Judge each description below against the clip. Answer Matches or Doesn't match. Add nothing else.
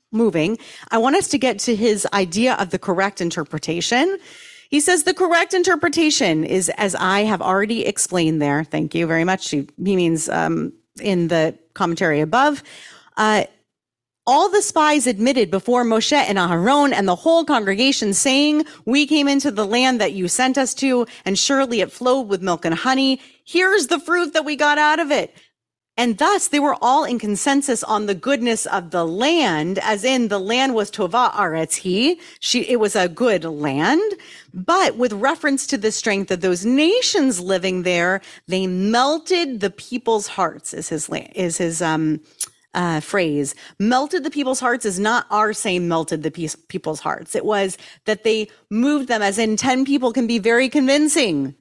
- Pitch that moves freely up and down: Matches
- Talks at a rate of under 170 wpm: Doesn't match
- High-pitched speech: Matches